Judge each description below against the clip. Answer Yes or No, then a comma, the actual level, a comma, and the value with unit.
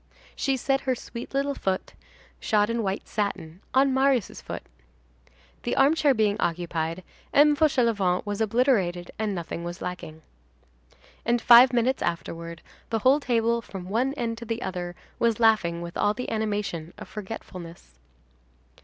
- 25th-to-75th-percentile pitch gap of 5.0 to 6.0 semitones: Yes, wide, 5.6 semitones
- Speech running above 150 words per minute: No, average, 145 wpm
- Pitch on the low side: No, high, 220 Hz